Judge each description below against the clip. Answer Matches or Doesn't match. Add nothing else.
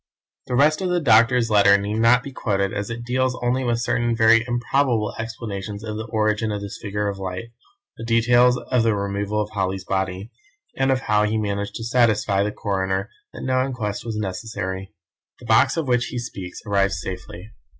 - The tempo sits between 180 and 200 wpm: Matches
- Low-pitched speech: Matches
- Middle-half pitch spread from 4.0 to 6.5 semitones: Doesn't match